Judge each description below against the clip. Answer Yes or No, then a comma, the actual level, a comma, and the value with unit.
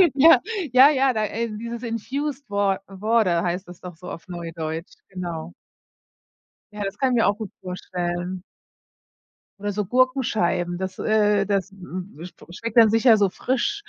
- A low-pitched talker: No, high, 205 Hz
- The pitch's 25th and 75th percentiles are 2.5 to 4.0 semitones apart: No, average, 4.4 semitones